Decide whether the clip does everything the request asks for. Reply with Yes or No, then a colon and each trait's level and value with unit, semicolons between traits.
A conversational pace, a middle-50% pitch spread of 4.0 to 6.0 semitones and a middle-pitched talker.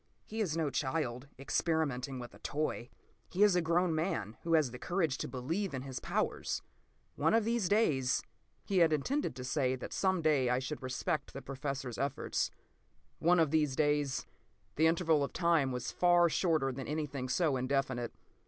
Yes: average, 180 wpm; average, 4.4 semitones; medium, 150 Hz